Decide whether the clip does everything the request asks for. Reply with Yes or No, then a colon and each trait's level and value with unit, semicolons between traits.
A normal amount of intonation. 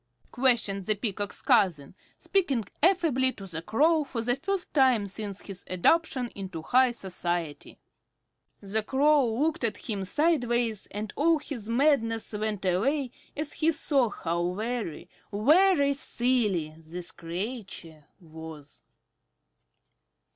No: wide, 6.5 semitones